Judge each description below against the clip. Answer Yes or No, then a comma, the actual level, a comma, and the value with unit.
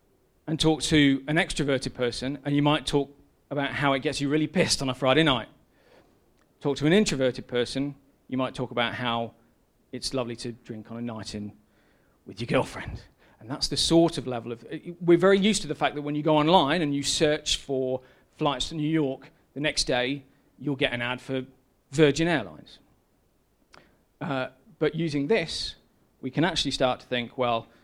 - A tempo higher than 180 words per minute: Yes, average, 190 wpm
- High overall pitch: No, medium, 140 Hz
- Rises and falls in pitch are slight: No, average, 3.6 semitones